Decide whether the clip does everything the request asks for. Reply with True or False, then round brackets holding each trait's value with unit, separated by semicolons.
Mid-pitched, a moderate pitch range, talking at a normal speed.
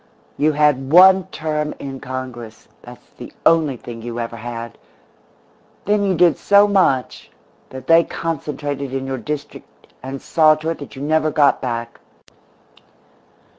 True (145 Hz; 3.7 semitones; 145 wpm)